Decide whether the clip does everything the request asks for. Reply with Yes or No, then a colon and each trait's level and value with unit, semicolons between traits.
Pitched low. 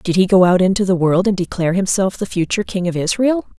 No: high, 190 Hz